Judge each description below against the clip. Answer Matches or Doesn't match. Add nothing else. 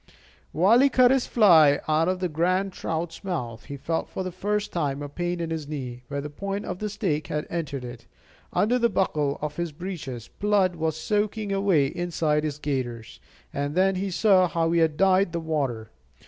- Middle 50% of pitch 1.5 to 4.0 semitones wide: Doesn't match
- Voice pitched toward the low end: Doesn't match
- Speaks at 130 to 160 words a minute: Doesn't match